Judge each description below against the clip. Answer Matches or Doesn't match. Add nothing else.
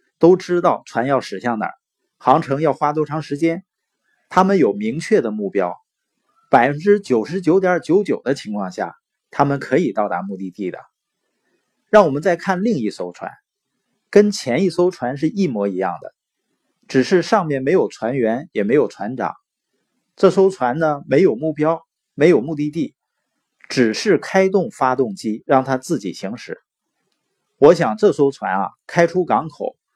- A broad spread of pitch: Matches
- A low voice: Doesn't match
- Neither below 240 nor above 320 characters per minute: Doesn't match